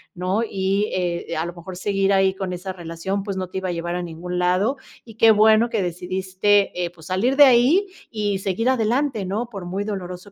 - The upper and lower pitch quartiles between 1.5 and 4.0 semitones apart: Yes, average, 3.2 semitones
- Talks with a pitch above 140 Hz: Yes, high, 190 Hz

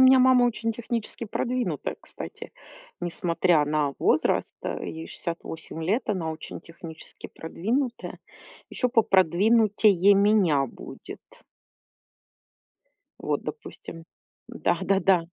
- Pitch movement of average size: No, wide, 5.7 semitones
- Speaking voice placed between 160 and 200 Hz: Yes, high, 195 Hz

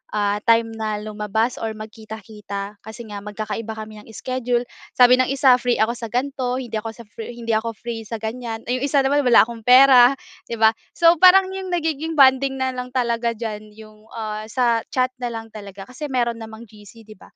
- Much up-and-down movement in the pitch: No, average, 2.7 semitones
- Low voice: No, high, 230 Hz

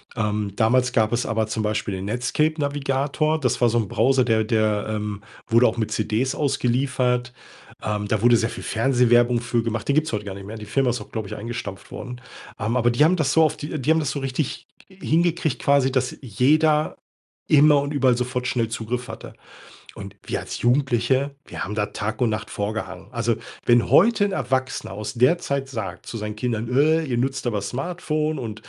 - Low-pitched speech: Yes, low, 125 Hz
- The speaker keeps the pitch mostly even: No, average, 4.1 semitones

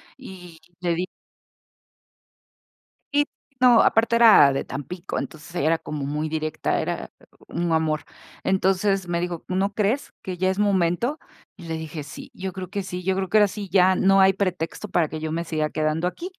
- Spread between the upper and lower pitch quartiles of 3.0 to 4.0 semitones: Yes, average, 3.4 semitones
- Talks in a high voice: No, medium, 180 Hz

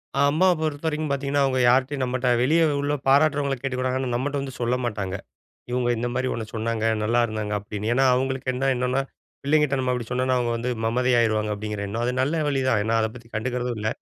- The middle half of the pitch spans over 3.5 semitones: No, average, 2.9 semitones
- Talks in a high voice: No, low, 125 Hz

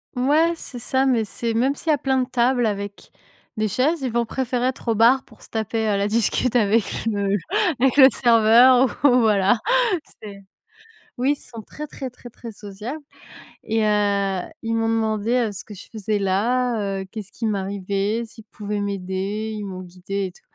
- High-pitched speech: Yes, high, 220 Hz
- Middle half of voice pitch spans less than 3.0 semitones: No, average, 3.6 semitones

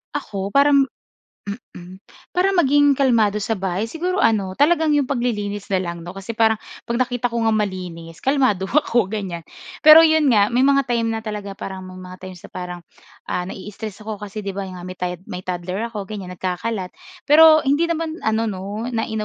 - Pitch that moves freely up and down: Yes, wide, 6.0 semitones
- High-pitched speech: Yes, high, 215 Hz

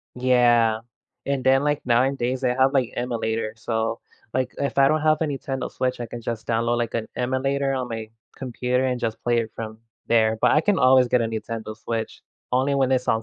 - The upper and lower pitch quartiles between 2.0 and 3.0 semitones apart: Yes, narrow, 2.5 semitones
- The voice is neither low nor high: No, low, 125 Hz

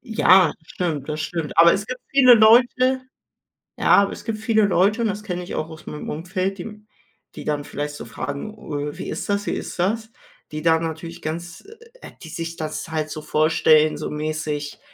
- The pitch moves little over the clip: No, wide, 5.4 semitones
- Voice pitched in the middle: Yes, medium, 170 Hz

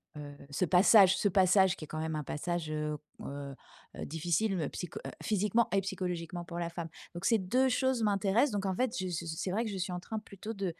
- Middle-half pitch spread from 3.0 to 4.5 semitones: Yes, average, 3.8 semitones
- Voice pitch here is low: No, medium, 185 Hz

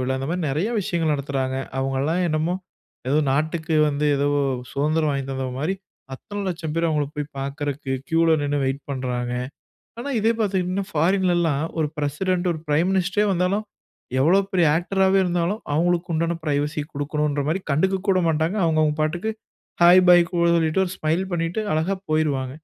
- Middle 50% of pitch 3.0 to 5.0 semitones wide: Yes, average, 3.7 semitones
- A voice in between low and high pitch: Yes, medium, 160 Hz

